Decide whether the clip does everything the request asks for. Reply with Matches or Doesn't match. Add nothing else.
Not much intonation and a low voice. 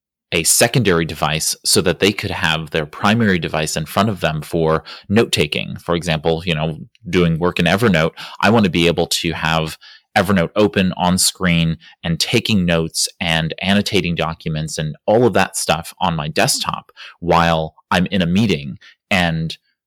Matches